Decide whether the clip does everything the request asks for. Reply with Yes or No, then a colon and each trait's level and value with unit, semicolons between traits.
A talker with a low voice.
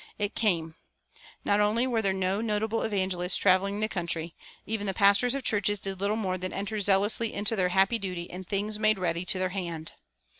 No: high, 200 Hz